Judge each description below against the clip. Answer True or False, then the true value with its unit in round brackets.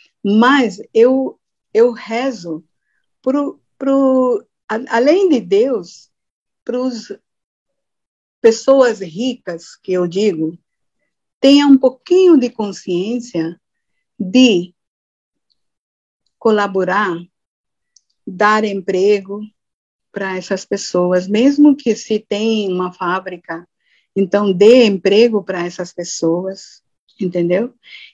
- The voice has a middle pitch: False (210 Hz)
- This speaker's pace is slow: True (85 wpm)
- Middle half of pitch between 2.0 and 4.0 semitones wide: False (5.2 semitones)